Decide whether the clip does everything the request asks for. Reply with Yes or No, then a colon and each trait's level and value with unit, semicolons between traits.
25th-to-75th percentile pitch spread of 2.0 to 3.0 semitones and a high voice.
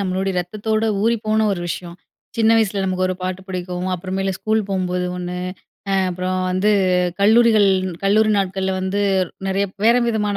Yes: average, 2.7 semitones; high, 195 Hz